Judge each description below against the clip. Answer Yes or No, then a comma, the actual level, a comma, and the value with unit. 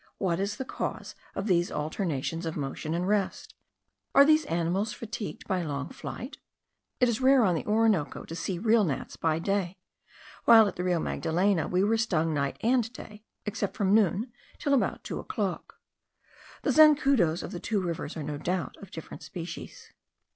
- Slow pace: No, average, 175 wpm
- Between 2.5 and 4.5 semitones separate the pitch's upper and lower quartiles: No, average, 5.1 semitones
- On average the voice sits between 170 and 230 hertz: Yes, high, 190 Hz